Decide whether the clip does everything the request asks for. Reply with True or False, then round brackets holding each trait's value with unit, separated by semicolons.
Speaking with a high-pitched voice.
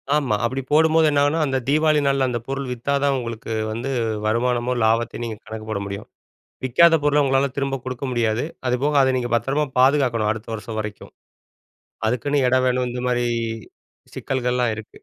False (125 Hz)